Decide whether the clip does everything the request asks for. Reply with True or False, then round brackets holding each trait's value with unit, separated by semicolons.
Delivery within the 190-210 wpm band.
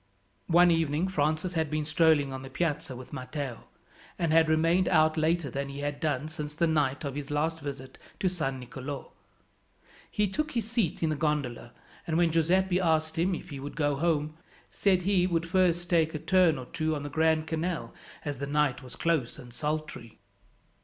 True (195 wpm)